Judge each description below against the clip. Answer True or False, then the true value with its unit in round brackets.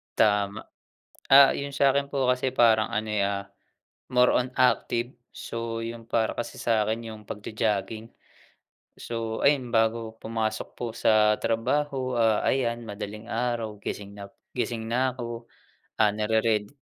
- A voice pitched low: True (115 Hz)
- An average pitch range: False (2.2 semitones)